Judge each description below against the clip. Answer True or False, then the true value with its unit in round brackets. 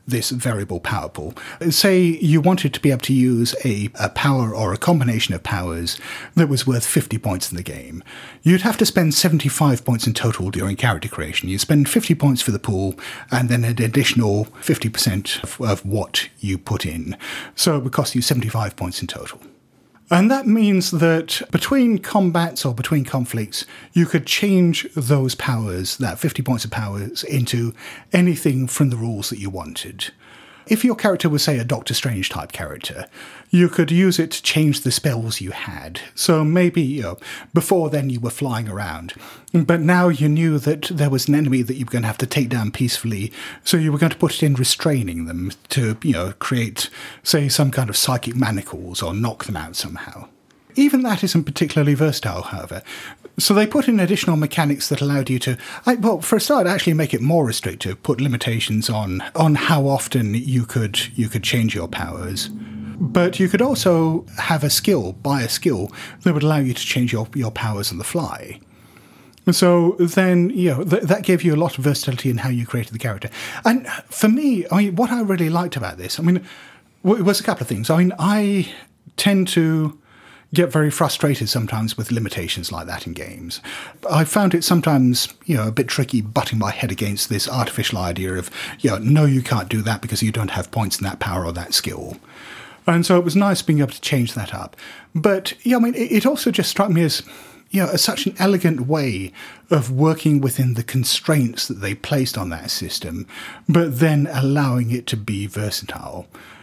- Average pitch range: False (7.3 semitones)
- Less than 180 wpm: False (205 wpm)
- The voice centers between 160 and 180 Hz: False (135 Hz)